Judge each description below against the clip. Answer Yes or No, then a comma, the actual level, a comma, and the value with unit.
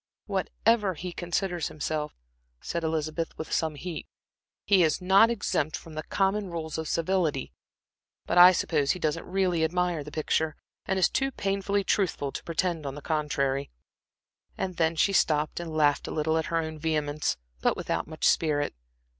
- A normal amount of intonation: Yes, average, 3.1 semitones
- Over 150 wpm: Yes, average, 170 wpm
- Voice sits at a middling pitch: Yes, medium, 165 Hz